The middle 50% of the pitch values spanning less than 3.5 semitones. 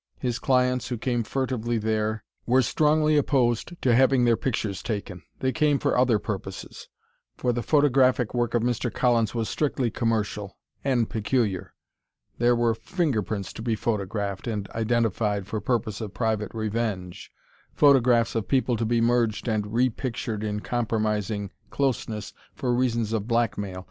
Yes: average, 2.8 semitones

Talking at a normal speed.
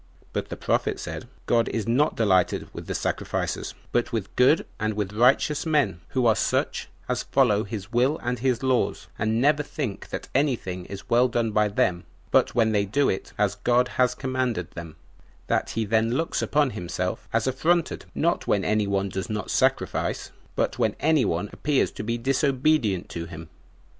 Yes: average, 185 wpm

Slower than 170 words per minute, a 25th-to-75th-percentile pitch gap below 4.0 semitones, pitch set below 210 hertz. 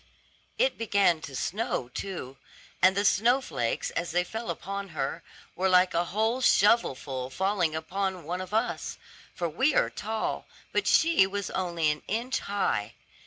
No: average, 160 wpm; average, 4.7 semitones; high, 190 Hz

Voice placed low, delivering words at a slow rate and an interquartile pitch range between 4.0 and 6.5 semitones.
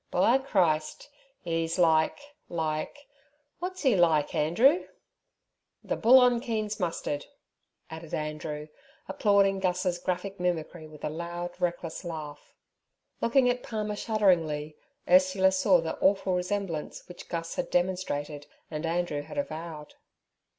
No: medium, 175 Hz; slow, 115 wpm; average, 4.7 semitones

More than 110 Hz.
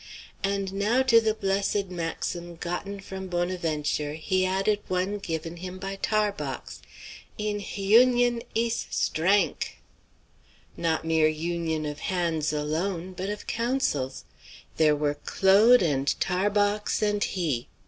Yes: medium, 185 Hz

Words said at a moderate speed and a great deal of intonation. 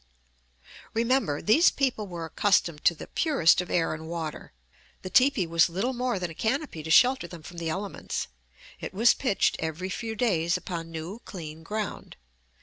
Yes: average, 170 wpm; wide, 5.7 semitones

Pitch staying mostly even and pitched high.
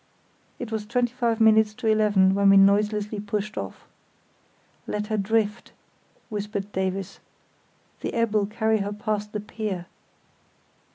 Yes: narrow, 1.5 semitones; high, 210 Hz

